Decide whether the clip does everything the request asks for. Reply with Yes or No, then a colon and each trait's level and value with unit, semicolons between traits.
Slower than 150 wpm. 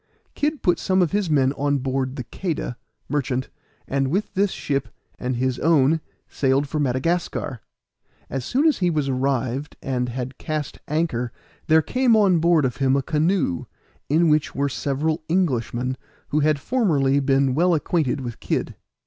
No: average, 165 wpm